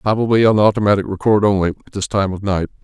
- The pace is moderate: No, fast, 210 wpm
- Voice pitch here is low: Yes, low, 100 Hz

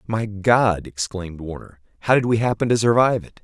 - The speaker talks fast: No, average, 190 wpm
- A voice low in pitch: Yes, low, 105 Hz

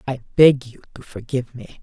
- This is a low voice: Yes, low, 130 Hz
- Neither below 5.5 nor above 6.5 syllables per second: Yes, 5.7 syllables/s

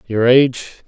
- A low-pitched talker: Yes, low, 125 Hz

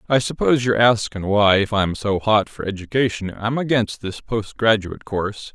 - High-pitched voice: No, low, 105 Hz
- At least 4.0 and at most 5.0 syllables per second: No, 5.2 syllables/s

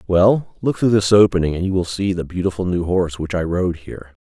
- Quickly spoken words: Yes, fast, 240 wpm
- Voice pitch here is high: No, very low, 90 Hz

